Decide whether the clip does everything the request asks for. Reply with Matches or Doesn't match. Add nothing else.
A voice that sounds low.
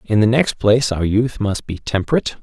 Matches